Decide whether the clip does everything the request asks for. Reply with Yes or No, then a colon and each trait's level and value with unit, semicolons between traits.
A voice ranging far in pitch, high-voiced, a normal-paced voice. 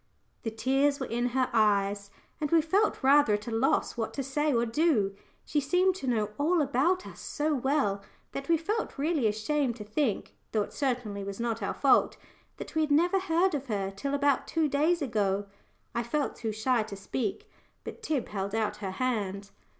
Yes: wide, 5.8 semitones; very high, 260 Hz; average, 195 wpm